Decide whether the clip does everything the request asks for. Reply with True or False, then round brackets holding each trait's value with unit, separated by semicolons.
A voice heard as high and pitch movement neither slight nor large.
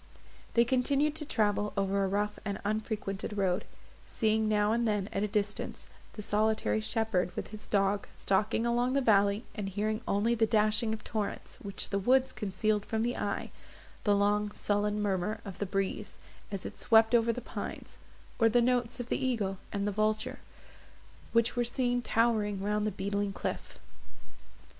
False (210 Hz; 2.2 semitones)